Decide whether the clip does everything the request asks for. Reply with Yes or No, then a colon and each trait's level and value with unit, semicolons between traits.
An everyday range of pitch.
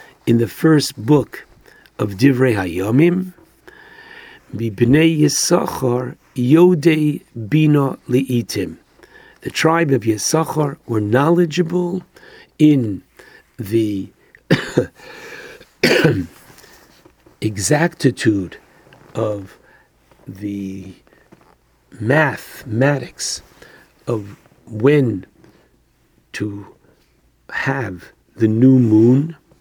No: wide, 6.4 semitones